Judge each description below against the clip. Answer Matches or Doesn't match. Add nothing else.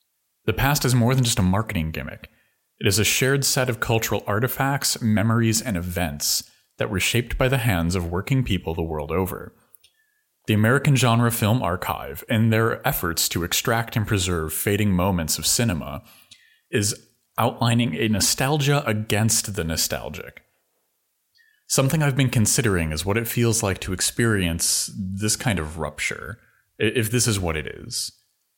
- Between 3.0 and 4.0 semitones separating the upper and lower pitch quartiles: Doesn't match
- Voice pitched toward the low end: Matches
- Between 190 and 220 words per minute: Doesn't match